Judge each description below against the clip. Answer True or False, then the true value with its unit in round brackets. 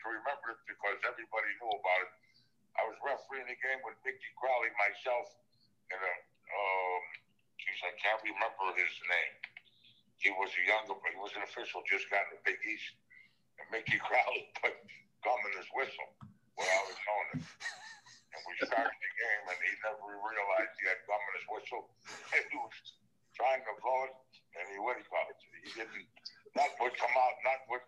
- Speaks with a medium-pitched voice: False (110 Hz)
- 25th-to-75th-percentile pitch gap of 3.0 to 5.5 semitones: True (3.4 semitones)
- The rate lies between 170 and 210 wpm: True (185 wpm)